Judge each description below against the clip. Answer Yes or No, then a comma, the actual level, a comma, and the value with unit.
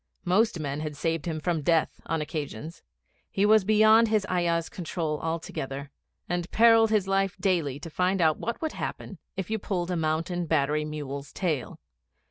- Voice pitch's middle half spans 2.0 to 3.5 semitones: No, average, 4.1 semitones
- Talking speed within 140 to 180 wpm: Yes, average, 170 wpm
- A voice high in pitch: No, medium, 170 Hz